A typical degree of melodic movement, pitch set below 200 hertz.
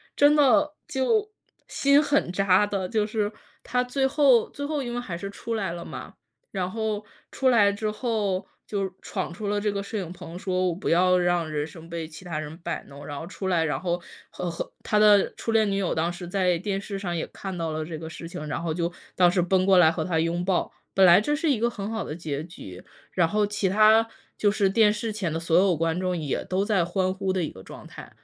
Yes: average, 3.9 semitones; high, 190 Hz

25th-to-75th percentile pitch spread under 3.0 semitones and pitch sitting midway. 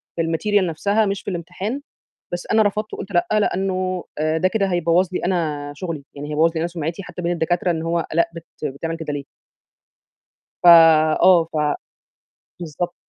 Yes: narrow, 2.5 semitones; medium, 170 Hz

